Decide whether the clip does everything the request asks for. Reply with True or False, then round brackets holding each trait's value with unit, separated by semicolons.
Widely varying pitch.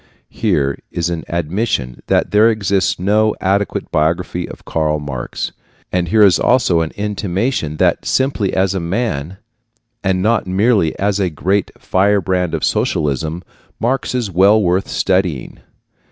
False (3.7 semitones)